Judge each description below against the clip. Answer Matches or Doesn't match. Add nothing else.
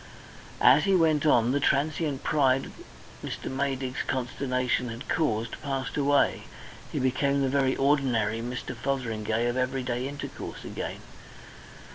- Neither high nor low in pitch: Doesn't match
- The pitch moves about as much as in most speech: Doesn't match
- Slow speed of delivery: Matches